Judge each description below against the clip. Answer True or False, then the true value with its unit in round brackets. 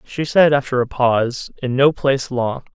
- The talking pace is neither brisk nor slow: True (195 wpm)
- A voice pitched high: False (130 Hz)